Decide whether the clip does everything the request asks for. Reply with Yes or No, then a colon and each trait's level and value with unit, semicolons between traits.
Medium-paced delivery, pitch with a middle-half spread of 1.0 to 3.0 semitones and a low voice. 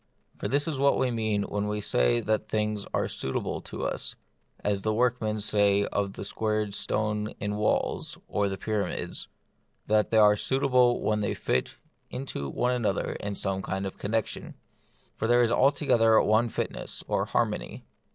Yes: average, 170 wpm; narrow, 2.4 semitones; low, 105 Hz